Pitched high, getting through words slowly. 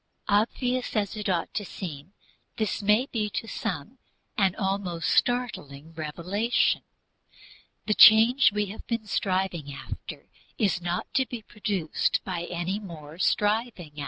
Yes: high, 200 Hz; slow, 130 wpm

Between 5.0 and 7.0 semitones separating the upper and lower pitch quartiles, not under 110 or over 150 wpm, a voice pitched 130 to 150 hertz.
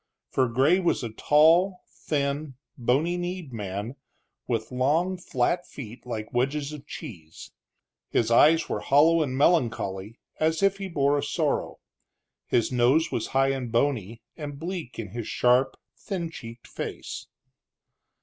Yes: wide, 5.4 semitones; average, 140 wpm; low, 135 Hz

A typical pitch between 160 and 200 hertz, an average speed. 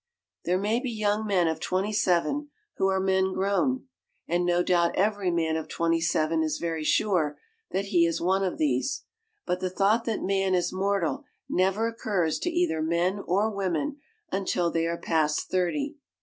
Yes: medium, 185 Hz; average, 180 wpm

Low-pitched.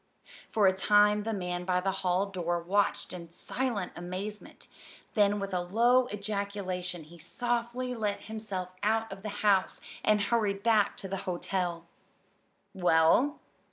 No: high, 200 Hz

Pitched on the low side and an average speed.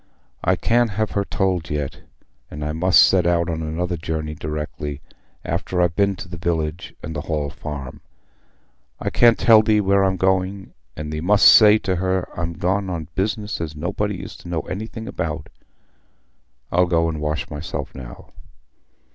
Yes: very low, 85 Hz; average, 170 wpm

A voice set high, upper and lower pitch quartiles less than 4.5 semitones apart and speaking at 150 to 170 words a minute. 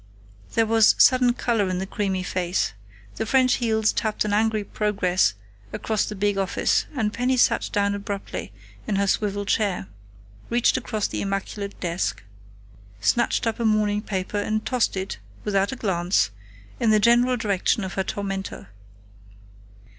Yes: high, 205 Hz; narrow, 2.5 semitones; average, 155 wpm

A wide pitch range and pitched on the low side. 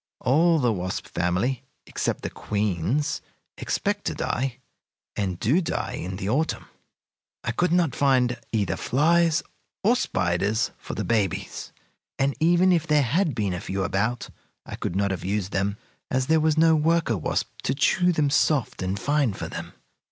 Yes: wide, 8.0 semitones; low, 125 Hz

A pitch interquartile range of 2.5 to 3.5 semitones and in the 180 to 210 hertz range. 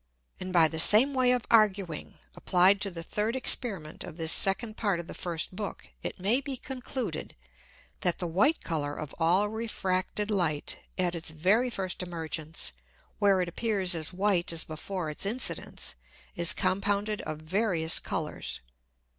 No: average, 4.2 semitones; medium, 185 Hz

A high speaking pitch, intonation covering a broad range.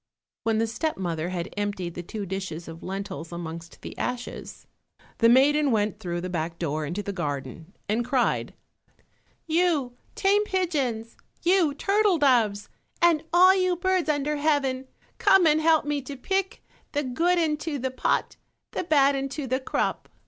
Yes: very high, 260 Hz; wide, 8.5 semitones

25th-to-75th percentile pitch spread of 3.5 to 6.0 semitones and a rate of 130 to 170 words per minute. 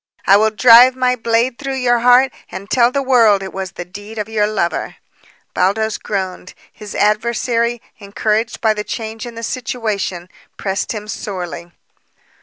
No: average, 3.1 semitones; average, 160 wpm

